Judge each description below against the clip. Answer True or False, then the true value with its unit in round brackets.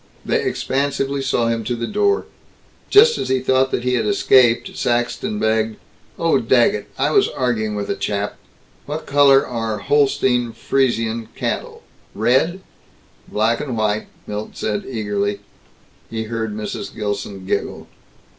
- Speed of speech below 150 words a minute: True (140 wpm)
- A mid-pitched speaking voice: False (120 Hz)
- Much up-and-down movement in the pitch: False (3.8 semitones)